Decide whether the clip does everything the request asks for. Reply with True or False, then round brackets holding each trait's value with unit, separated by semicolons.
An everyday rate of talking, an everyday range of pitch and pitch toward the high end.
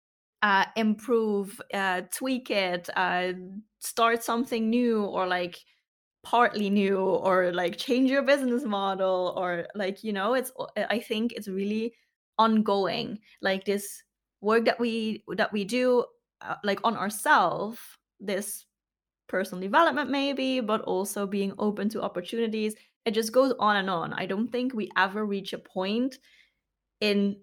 True (145 wpm; 3.5 semitones; 210 Hz)